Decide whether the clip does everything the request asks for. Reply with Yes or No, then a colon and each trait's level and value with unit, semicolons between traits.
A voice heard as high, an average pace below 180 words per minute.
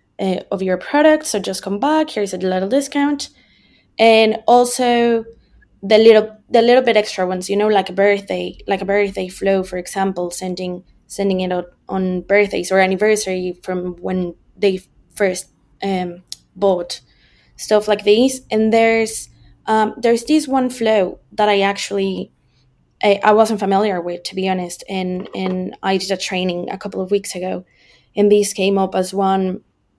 Yes: high, 195 Hz; average, 170 wpm